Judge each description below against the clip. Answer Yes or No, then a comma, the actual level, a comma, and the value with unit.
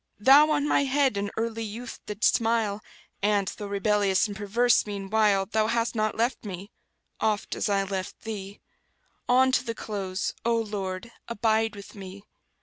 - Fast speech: No, average, 160 wpm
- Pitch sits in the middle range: No, high, 215 Hz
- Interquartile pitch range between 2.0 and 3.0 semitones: Yes, narrow, 2.5 semitones